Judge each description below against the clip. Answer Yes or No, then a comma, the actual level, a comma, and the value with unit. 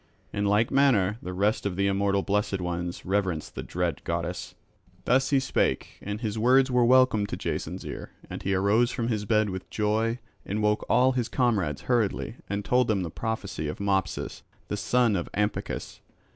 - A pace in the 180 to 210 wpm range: Yes, average, 185 wpm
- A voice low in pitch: Yes, low, 105 Hz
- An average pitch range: Yes, average, 3.4 semitones